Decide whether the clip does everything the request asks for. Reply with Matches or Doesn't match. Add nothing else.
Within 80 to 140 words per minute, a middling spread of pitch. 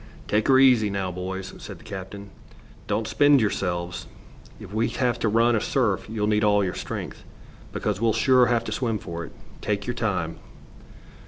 Doesn't match